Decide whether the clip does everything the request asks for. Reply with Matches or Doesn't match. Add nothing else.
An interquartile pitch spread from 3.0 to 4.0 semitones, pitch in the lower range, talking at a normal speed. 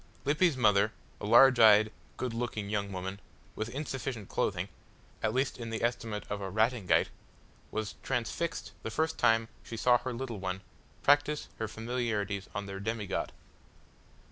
Matches